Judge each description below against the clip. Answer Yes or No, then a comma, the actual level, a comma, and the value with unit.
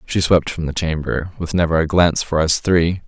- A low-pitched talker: Yes, very low, 85 Hz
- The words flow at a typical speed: No, fast, 215 wpm